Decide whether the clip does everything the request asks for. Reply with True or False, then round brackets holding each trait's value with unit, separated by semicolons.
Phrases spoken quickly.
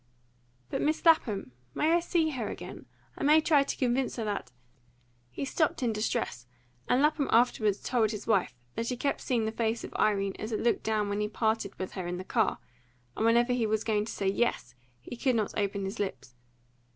True (210 wpm)